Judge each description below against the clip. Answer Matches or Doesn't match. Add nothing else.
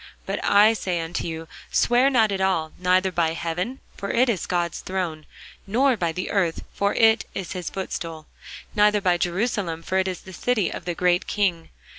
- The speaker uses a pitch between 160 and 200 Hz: Matches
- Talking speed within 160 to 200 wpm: Matches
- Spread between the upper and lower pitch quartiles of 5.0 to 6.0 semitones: Doesn't match